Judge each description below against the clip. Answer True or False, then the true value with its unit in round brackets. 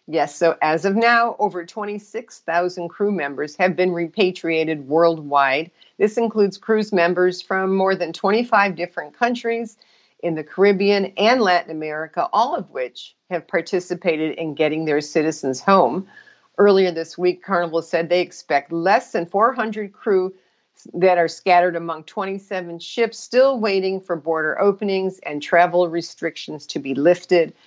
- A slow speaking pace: False (145 wpm)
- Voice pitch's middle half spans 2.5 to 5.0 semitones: True (3.3 semitones)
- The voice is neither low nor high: True (180 Hz)